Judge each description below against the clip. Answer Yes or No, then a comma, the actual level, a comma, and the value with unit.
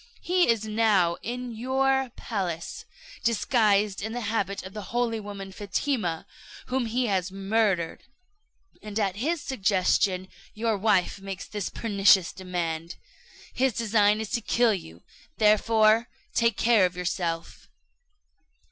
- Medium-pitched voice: No, high, 210 Hz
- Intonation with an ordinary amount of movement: Yes, average, 3.4 semitones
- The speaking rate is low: Yes, slow, 125 wpm